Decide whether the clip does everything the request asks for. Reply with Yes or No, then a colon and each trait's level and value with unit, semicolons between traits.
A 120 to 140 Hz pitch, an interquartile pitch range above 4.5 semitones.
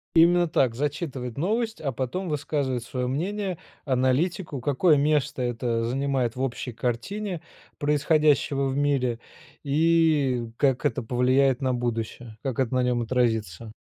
No: low, 135 Hz; average, 3.6 semitones